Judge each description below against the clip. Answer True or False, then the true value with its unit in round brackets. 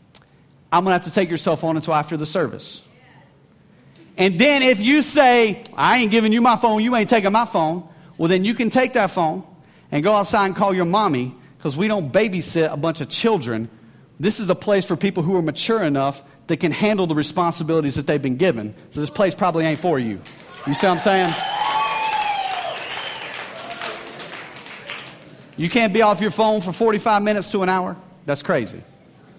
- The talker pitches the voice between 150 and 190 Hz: True (185 Hz)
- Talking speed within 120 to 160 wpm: False (195 wpm)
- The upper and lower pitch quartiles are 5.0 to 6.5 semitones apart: True (5.4 semitones)